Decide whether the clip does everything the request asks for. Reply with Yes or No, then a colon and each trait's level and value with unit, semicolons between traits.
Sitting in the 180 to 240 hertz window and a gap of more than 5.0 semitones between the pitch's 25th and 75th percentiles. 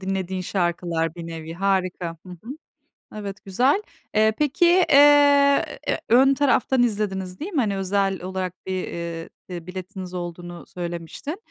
Yes: high, 190 Hz; wide, 5.6 semitones